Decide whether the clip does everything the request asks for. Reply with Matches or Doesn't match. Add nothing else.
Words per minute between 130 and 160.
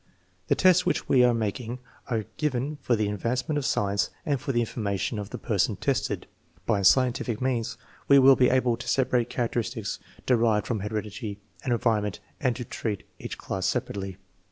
Doesn't match